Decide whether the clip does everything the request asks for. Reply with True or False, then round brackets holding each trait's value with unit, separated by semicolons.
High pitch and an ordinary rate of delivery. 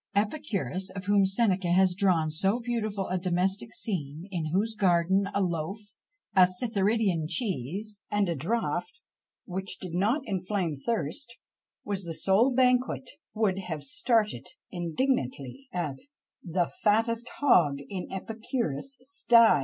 False (195 Hz; 130 wpm)